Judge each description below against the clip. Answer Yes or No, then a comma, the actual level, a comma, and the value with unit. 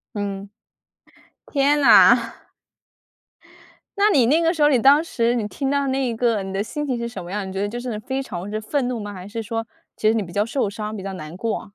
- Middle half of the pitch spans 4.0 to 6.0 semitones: Yes, average, 4.9 semitones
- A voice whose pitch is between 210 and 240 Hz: Yes, high, 230 Hz